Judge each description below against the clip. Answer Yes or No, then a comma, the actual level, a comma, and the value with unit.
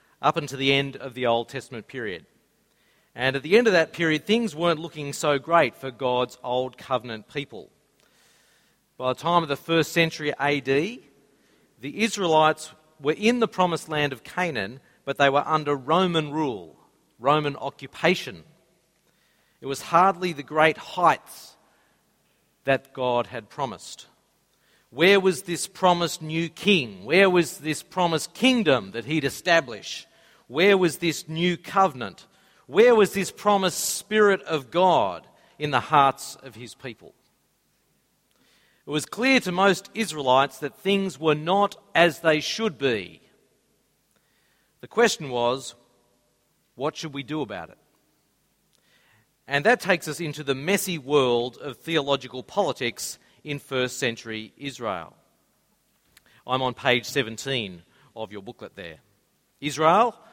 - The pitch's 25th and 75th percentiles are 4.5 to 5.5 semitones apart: Yes, average, 4.8 semitones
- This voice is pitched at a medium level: Yes, medium, 155 Hz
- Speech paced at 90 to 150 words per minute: Yes, average, 140 wpm